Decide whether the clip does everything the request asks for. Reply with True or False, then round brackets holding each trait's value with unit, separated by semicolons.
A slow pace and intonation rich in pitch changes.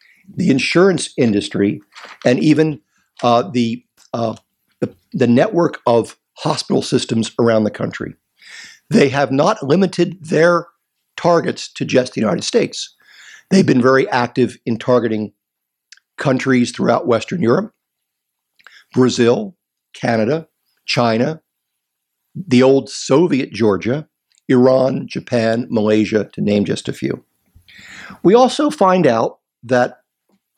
True (115 wpm; 6.4 semitones)